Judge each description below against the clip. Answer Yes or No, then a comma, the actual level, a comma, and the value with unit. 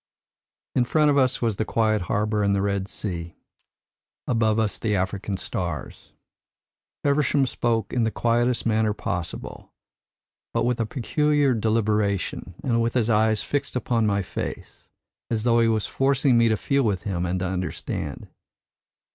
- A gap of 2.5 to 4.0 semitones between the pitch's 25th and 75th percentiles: Yes, average, 3.1 semitones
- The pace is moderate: Yes, average, 155 wpm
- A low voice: Yes, low, 110 Hz